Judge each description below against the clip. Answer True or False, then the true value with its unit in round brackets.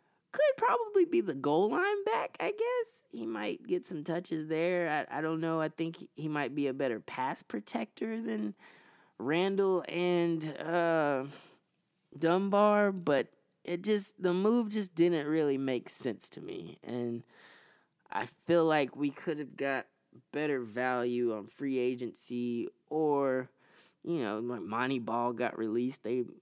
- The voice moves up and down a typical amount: False (6.0 semitones)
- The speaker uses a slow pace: False (155 wpm)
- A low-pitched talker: False (155 Hz)